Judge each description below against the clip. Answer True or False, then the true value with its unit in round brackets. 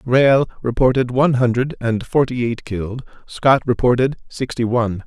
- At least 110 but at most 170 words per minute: True (140 wpm)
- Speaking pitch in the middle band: False (125 Hz)